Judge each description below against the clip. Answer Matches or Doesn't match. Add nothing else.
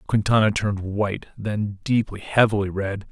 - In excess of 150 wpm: Doesn't match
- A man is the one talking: Matches